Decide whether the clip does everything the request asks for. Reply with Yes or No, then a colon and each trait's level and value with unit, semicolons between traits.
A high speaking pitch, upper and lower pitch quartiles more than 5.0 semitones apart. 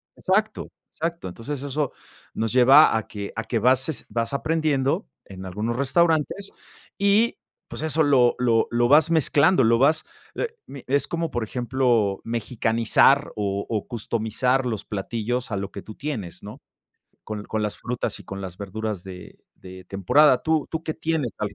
No: low, 125 Hz; wide, 5.5 semitones